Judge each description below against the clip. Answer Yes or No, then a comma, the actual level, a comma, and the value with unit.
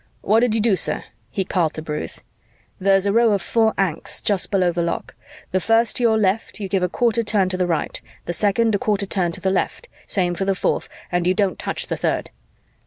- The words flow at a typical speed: No, fast, 235 wpm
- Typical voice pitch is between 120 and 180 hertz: No, high, 195 Hz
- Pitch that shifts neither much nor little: Yes, average, 3.3 semitones